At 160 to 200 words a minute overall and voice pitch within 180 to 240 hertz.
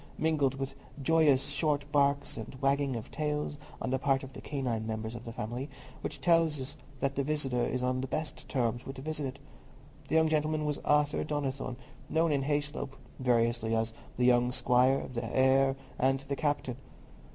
No: average, 175 wpm; low, 135 Hz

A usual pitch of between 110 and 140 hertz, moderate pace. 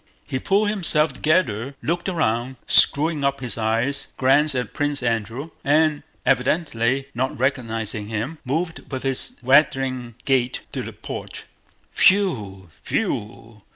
No: low, 135 Hz; slow, 125 wpm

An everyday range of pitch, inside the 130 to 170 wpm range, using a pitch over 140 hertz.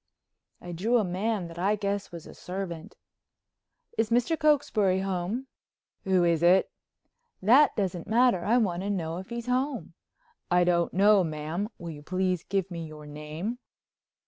Yes: average, 4.2 semitones; average, 160 wpm; high, 190 Hz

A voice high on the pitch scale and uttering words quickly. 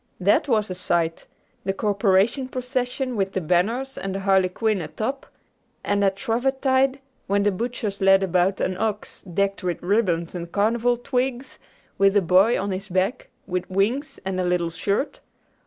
No: high, 200 Hz; average, 160 wpm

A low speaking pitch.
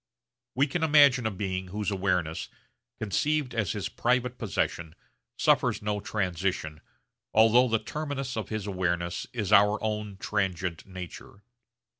Yes: low, 105 Hz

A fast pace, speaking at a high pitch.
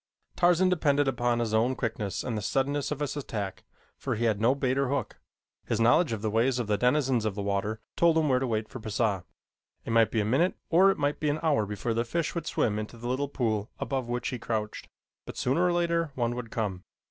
No: fast, 240 wpm; low, 120 Hz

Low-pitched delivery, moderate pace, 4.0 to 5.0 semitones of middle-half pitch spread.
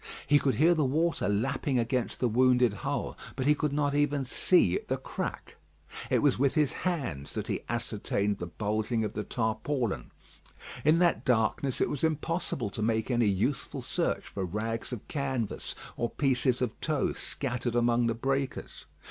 Yes: low, 125 Hz; average, 175 wpm; average, 4.4 semitones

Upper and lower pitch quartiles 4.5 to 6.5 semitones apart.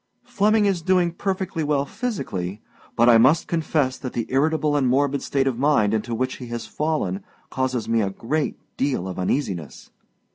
Yes: average, 5.3 semitones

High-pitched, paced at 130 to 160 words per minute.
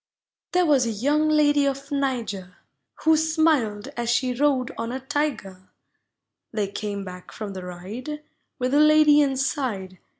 Yes: very high, 260 Hz; average, 145 wpm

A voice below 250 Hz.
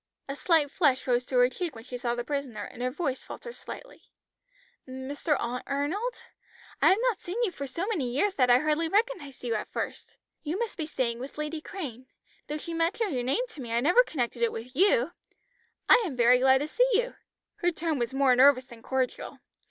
No: very high, 280 Hz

